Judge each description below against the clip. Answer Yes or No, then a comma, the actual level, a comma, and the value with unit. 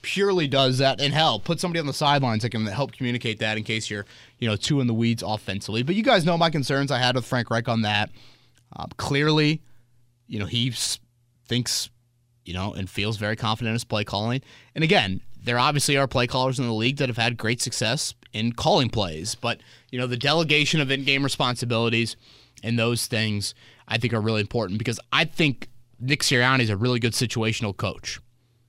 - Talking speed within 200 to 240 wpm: Yes, fast, 205 wpm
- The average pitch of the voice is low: Yes, low, 120 Hz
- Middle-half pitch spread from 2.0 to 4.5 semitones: Yes, average, 3.1 semitones